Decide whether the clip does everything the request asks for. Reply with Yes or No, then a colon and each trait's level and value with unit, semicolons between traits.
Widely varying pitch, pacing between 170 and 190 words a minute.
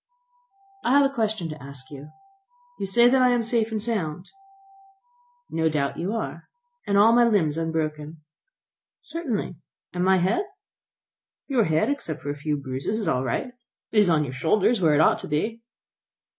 Yes: wide, 7.0 semitones; average, 180 wpm